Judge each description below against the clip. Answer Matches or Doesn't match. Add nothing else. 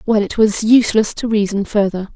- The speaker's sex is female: Matches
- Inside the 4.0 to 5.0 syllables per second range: Doesn't match